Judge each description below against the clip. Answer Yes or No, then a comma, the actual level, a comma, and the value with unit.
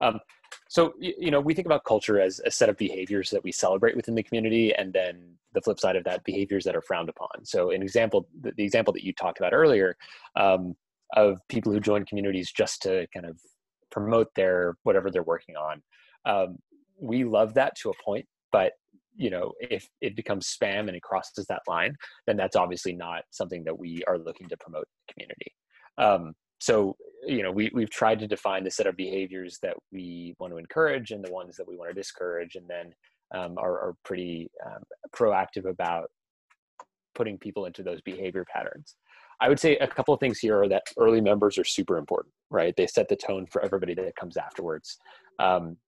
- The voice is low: Yes, low, 105 Hz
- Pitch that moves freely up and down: Yes, wide, 6.7 semitones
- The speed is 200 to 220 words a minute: Yes, fast, 205 wpm